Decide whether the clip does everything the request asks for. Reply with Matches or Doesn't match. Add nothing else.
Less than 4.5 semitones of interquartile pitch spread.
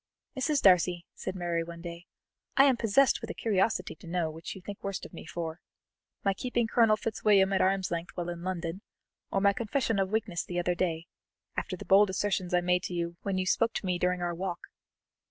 Matches